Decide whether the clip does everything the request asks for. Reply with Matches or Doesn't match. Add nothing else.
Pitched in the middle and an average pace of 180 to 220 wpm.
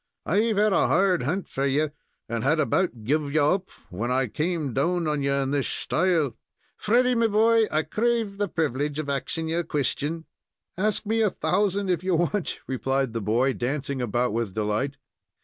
Matches